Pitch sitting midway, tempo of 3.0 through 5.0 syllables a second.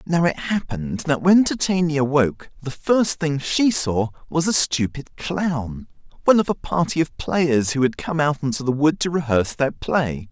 Yes: medium, 150 Hz; 4.6 syllables/s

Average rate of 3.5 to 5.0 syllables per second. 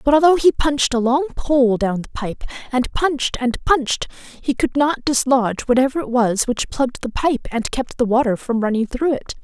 No: 5.2 syllables/s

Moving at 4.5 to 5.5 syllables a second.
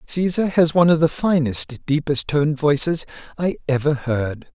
Yes: 4.8 syllables/s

